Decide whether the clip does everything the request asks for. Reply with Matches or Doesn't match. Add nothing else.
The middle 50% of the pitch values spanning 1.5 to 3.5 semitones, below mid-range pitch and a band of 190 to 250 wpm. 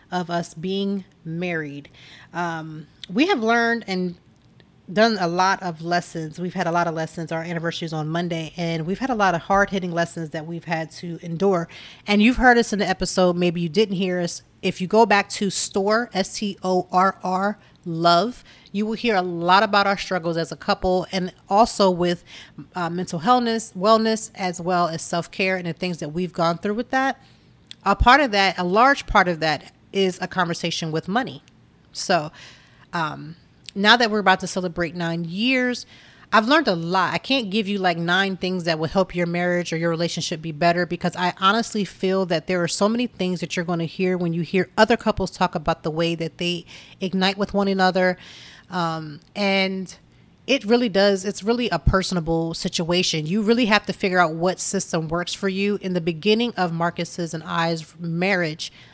Doesn't match